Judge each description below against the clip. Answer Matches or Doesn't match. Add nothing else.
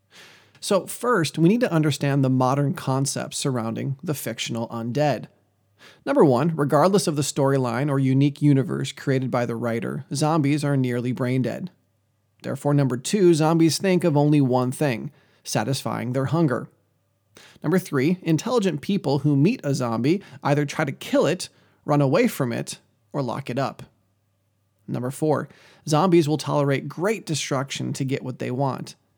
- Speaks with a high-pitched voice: Doesn't match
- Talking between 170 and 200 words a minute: Doesn't match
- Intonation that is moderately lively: Matches